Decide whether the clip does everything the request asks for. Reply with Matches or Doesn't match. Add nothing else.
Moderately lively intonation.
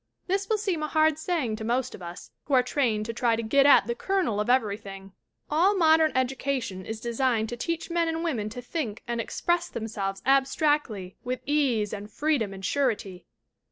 Doesn't match